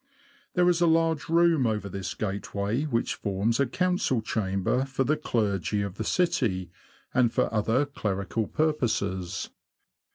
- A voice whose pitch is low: Yes, low, 115 Hz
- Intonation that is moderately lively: No, wide, 7.3 semitones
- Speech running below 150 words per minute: Yes, average, 140 wpm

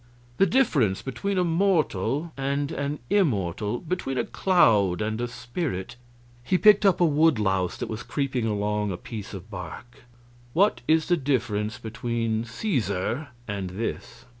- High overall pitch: No, low, 120 Hz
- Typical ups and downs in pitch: No, wide, 7.2 semitones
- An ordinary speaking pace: Yes, average, 150 wpm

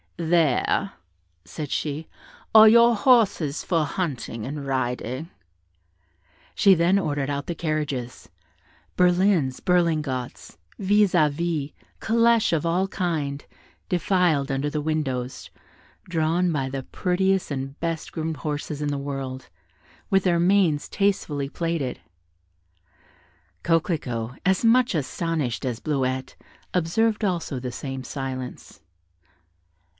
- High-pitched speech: No, medium, 155 Hz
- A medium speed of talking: No, slow, 110 wpm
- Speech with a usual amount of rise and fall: Yes, average, 4.8 semitones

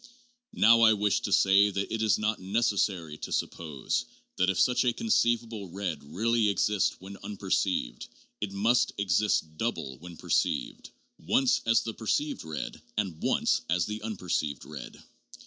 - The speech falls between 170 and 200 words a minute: No, average, 155 wpm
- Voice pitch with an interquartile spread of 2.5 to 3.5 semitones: No, average, 3.9 semitones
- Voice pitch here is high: No, low, 100 Hz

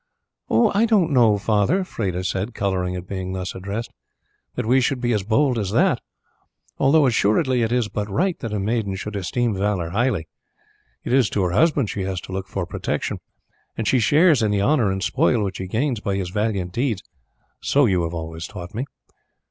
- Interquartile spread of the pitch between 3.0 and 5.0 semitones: Yes, average, 4.6 semitones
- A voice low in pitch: Yes, low, 105 Hz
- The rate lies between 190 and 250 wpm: Yes, average, 195 wpm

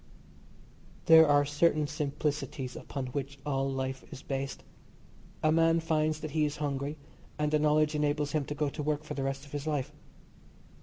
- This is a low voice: No, medium, 150 Hz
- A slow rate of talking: No, average, 175 wpm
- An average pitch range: No, narrow, 1.7 semitones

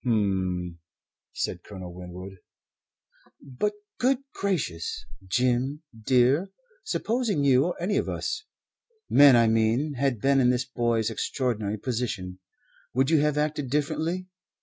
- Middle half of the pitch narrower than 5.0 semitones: No, wide, 5.5 semitones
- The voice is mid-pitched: No, low, 130 Hz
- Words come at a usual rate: No, slow, 125 wpm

